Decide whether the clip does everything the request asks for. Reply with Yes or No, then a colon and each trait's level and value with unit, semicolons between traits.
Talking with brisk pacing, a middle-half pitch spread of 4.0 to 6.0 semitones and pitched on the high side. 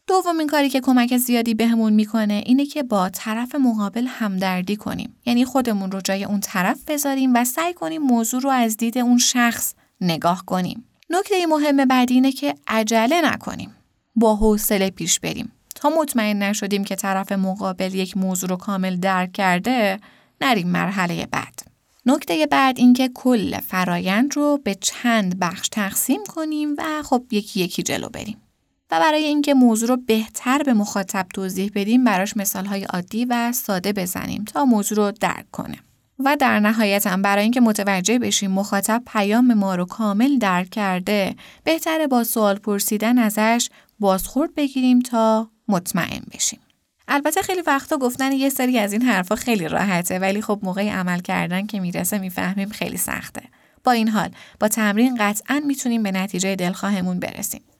Yes: fast, 160 wpm; average, 4.4 semitones; high, 220 Hz